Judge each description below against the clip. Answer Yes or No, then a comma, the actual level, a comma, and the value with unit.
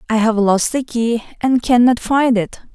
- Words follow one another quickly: No, average, 195 wpm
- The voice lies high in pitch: Yes, high, 235 Hz